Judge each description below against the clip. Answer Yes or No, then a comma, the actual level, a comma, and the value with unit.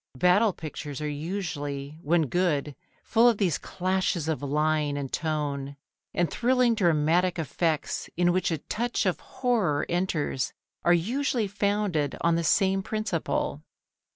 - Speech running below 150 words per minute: Yes, slow, 135 wpm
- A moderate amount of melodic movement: Yes, average, 4.9 semitones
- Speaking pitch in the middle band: Yes, medium, 170 Hz